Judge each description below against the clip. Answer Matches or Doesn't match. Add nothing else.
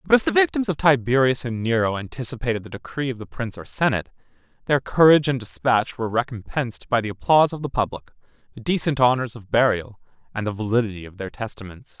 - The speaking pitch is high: Doesn't match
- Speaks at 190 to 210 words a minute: Matches